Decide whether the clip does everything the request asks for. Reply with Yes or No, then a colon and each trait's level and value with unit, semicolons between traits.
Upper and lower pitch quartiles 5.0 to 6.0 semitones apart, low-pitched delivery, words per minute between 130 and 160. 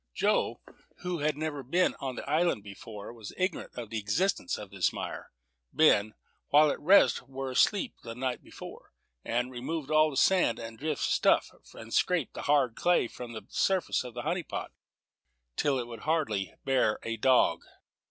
No: average, 5.3 semitones; low, 130 Hz; average, 175 wpm